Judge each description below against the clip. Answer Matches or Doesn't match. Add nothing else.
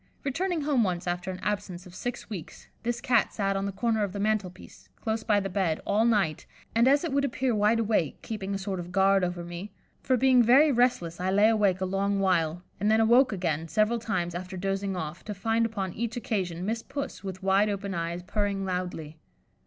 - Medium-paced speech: Doesn't match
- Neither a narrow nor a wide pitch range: Matches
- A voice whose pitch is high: Matches